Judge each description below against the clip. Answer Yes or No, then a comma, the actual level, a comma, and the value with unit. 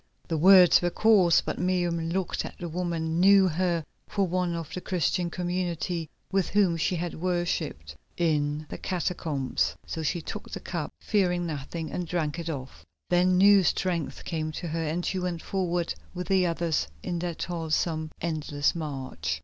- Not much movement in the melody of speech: Yes, narrow, 2.2 semitones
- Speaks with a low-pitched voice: No, medium, 170 Hz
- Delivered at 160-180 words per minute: Yes, average, 170 wpm